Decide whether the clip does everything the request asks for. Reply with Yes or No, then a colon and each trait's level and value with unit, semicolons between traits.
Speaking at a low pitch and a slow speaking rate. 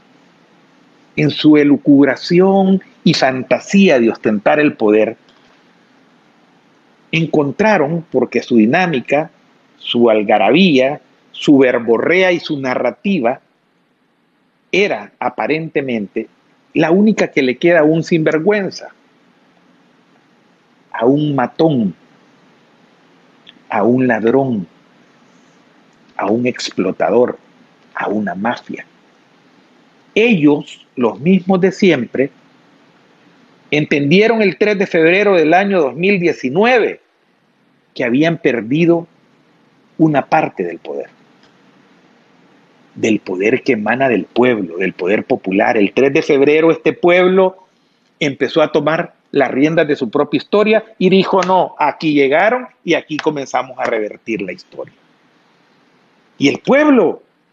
No: medium, 160 Hz; slow, 105 wpm